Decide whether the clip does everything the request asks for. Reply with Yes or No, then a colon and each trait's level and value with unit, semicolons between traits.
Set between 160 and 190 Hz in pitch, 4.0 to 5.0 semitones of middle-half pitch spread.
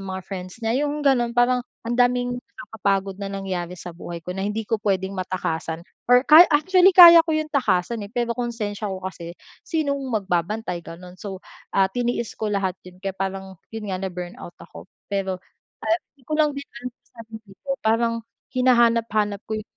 No: high, 210 Hz; average, 4.6 semitones